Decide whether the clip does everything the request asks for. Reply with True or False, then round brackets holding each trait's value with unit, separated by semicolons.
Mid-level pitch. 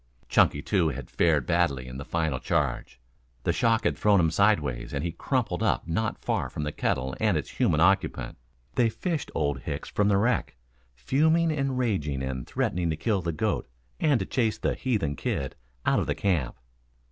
False (85 Hz)